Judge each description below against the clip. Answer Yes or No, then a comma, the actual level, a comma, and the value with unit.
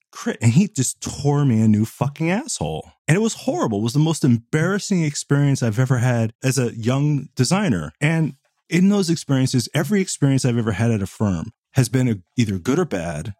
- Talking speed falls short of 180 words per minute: No, fast, 205 wpm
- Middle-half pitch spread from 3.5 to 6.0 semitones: Yes, average, 5.3 semitones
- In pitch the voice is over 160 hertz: No, low, 130 Hz